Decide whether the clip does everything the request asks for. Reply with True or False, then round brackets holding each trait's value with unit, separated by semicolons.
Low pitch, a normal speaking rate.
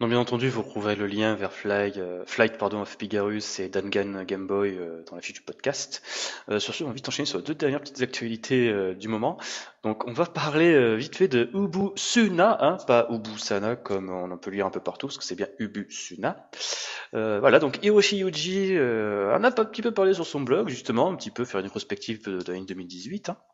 False (110 Hz; 235 wpm)